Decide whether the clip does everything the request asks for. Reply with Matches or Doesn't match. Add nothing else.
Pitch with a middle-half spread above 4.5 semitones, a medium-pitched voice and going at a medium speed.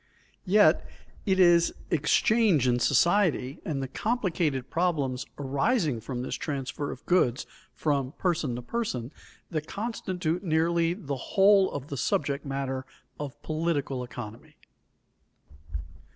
Doesn't match